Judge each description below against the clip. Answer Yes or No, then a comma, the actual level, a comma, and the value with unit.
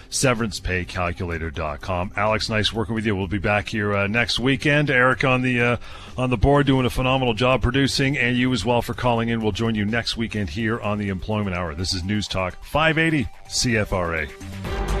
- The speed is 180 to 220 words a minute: Yes, average, 190 wpm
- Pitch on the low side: Yes, low, 110 Hz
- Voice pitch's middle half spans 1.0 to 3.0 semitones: No, average, 4.3 semitones